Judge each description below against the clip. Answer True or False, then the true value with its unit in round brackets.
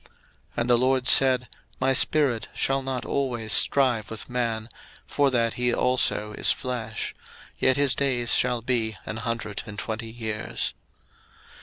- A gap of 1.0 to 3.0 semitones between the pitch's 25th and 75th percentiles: True (2.6 semitones)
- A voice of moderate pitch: False (120 Hz)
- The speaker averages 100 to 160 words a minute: True (150 wpm)